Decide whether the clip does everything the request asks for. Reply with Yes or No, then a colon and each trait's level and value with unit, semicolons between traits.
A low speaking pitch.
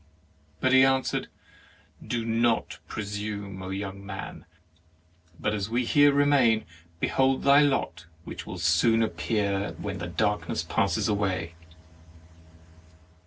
Yes: low, 105 Hz